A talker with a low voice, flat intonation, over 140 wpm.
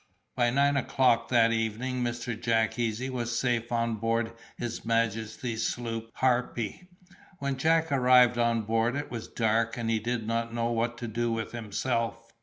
Yes: low, 115 Hz; narrow, 1.4 semitones; average, 165 wpm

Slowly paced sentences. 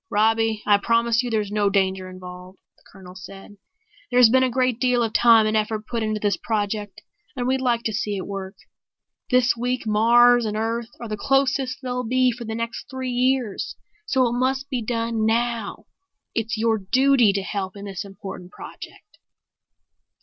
No: average, 180 wpm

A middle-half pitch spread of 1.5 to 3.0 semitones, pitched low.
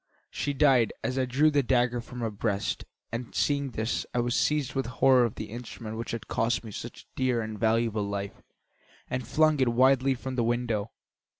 Yes: average, 2.7 semitones; low, 120 Hz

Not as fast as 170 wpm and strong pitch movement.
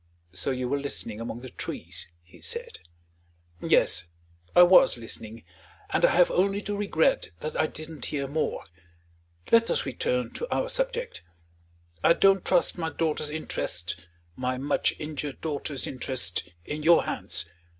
Yes: average, 150 wpm; wide, 5.8 semitones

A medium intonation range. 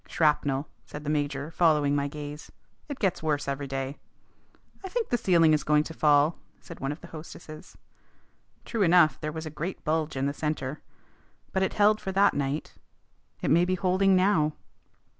Yes: average, 3.7 semitones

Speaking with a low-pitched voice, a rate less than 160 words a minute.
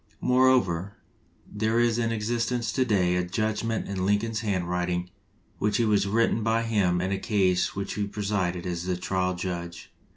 No: low, 100 Hz; average, 165 wpm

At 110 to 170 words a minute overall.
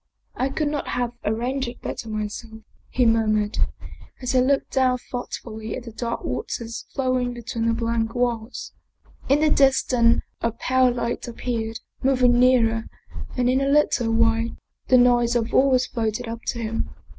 No: average, 180 wpm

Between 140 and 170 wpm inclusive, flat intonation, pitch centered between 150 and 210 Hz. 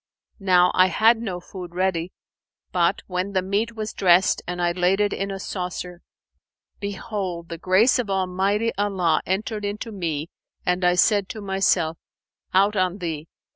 Yes: average, 160 wpm; narrow, 2.3 semitones; medium, 185 Hz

